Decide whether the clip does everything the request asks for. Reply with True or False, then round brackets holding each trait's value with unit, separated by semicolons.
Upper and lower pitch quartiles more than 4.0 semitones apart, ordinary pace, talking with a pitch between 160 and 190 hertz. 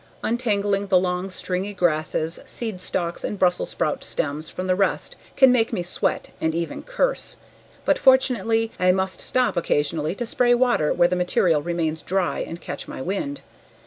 True (4.8 semitones; 170 wpm; 185 Hz)